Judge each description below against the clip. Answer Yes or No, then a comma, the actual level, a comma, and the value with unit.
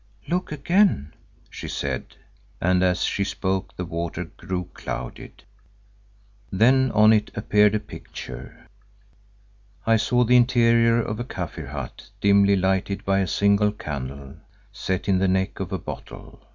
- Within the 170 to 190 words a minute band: No, average, 140 wpm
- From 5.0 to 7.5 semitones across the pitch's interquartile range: No, average, 3.8 semitones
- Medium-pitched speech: No, low, 100 Hz